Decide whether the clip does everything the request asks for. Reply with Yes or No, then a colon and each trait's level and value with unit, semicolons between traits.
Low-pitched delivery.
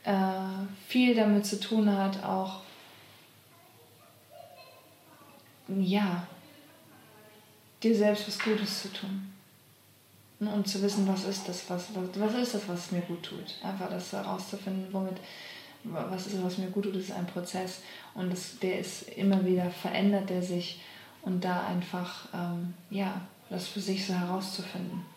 No: high, 190 Hz